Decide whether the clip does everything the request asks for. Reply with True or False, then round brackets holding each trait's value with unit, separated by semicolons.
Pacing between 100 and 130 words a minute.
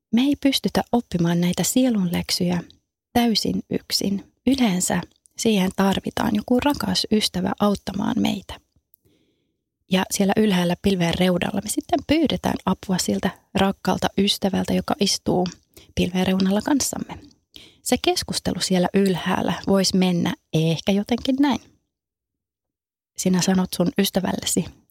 True (110 wpm)